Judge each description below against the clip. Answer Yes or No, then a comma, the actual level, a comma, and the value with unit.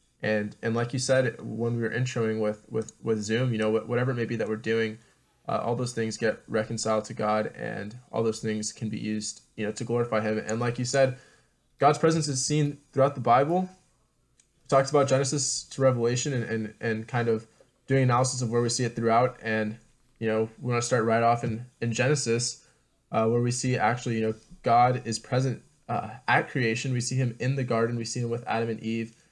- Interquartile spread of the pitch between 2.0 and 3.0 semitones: Yes, narrow, 2.5 semitones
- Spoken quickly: Yes, fast, 225 wpm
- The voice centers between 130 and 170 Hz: No, low, 115 Hz